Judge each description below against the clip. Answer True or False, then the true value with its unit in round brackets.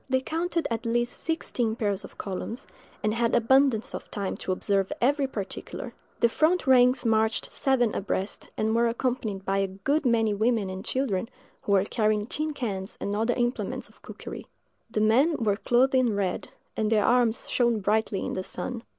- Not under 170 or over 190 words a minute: True (180 wpm)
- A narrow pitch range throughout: False (3.5 semitones)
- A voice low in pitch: False (230 Hz)